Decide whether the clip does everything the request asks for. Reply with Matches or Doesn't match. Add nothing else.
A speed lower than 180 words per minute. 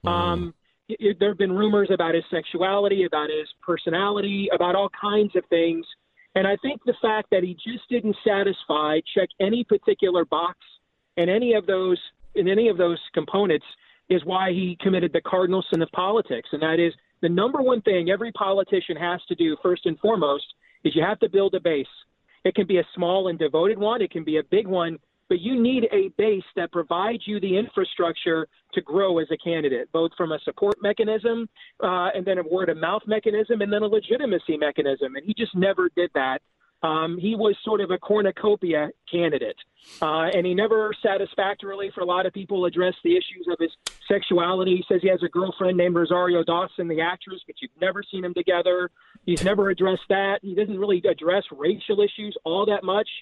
Doesn't match